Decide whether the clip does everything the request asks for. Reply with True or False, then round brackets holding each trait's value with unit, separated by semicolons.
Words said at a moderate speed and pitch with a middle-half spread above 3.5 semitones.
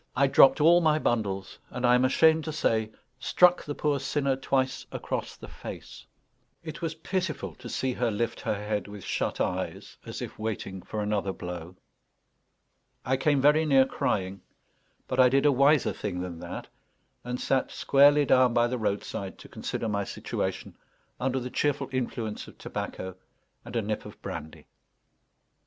True (170 wpm; 5.2 semitones)